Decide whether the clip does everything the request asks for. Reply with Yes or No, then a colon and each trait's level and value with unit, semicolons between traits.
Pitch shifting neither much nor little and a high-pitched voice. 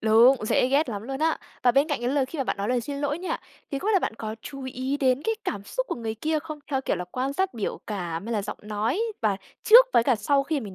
Yes: average, 4.9 semitones; very high, 260 Hz